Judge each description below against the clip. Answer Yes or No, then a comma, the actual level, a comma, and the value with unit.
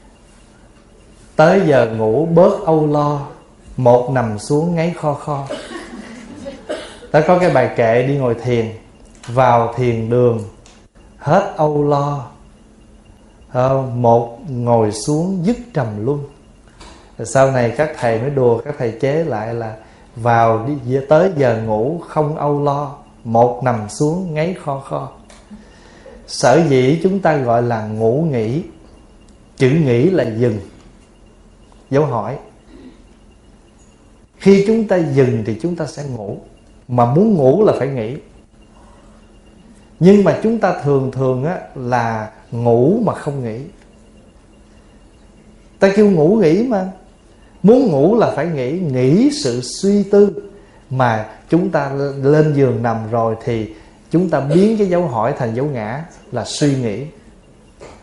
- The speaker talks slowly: Yes, slow, 135 wpm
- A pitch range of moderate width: No, wide, 6.0 semitones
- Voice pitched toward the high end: No, low, 135 Hz